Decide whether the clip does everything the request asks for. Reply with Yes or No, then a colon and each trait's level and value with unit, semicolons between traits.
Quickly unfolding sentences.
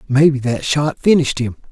No: average, 175 wpm